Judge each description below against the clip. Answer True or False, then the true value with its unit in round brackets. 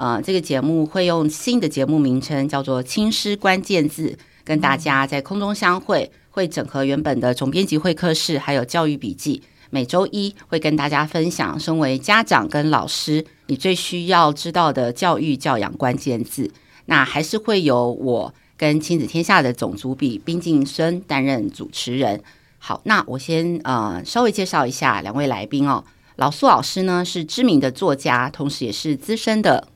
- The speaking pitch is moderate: True (155 Hz)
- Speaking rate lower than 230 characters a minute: False (270 characters per minute)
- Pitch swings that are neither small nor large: True (4.5 semitones)